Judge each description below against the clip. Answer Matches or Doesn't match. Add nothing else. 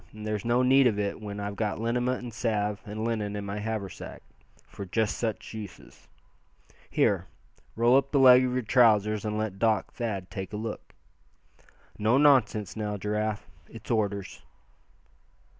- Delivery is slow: Doesn't match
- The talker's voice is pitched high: Doesn't match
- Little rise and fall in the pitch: Matches